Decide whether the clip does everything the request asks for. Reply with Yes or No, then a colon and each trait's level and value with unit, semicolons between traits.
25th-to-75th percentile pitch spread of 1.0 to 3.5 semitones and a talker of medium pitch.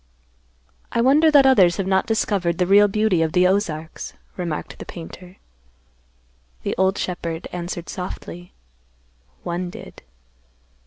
Yes: average, 2.9 semitones; medium, 180 Hz